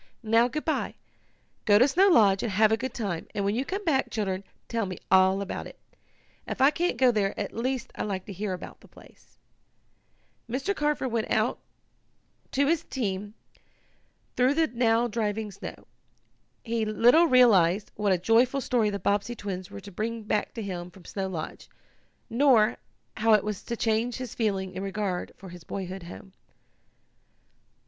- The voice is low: No, high, 215 Hz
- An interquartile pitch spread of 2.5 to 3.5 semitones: No, average, 3.9 semitones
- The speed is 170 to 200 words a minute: Yes, average, 175 wpm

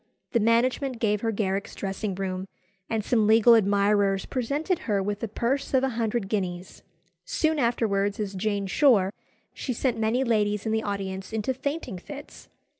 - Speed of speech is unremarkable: Yes, average, 165 wpm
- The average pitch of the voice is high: Yes, high, 215 Hz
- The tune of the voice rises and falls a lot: No, average, 3.3 semitones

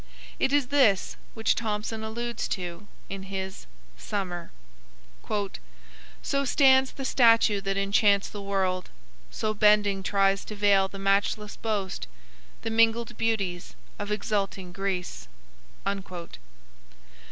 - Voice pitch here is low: No, high, 205 Hz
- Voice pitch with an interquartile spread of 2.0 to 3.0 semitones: Yes, narrow, 2.5 semitones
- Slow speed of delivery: Yes, slow, 110 wpm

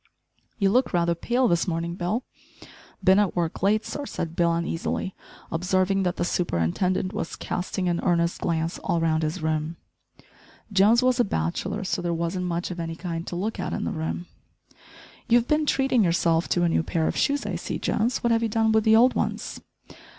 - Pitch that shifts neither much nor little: Yes, average, 4.4 semitones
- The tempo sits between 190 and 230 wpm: Yes, average, 195 wpm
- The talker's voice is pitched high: No, medium, 180 Hz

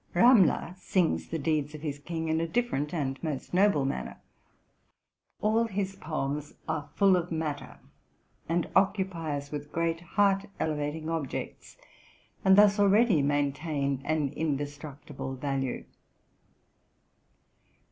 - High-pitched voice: No, medium, 160 Hz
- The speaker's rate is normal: No, slow, 125 wpm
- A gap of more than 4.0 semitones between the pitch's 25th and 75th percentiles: Yes, average, 4.7 semitones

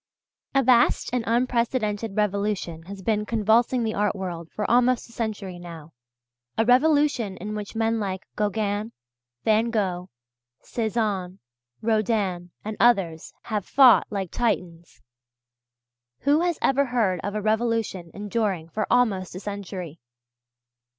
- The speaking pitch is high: Yes, high, 210 Hz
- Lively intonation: No, average, 3.6 semitones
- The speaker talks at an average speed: No, slow, 130 wpm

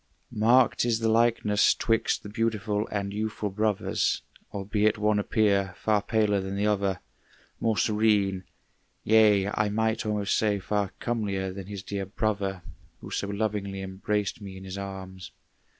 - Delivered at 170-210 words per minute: No, average, 150 wpm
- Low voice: Yes, low, 105 Hz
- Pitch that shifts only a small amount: Yes, narrow, 1.8 semitones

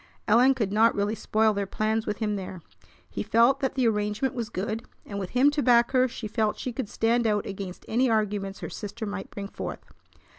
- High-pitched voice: Yes, high, 220 Hz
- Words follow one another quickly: Yes, fast, 215 wpm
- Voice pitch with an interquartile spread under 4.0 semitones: Yes, average, 2.8 semitones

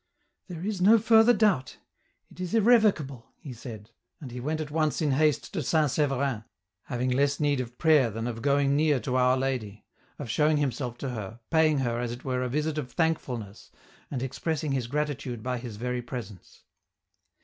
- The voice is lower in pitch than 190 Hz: Yes, low, 135 Hz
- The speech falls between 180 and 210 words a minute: Yes, average, 195 wpm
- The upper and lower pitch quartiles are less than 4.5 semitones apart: Yes, average, 4.1 semitones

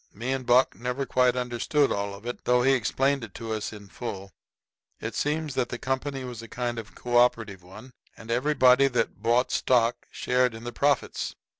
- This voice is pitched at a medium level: No, low, 125 Hz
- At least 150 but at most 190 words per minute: Yes, average, 185 wpm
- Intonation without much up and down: Yes, narrow, 2.3 semitones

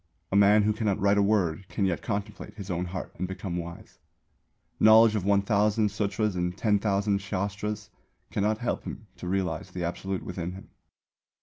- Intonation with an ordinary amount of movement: No, narrow, 2.2 semitones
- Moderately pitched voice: No, low, 100 Hz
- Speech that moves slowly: No, average, 170 wpm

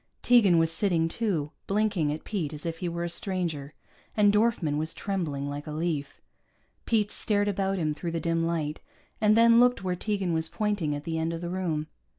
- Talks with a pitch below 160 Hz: No, medium, 170 Hz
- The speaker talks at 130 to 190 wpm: No, average, 200 wpm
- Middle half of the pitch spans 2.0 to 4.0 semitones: No, average, 4.4 semitones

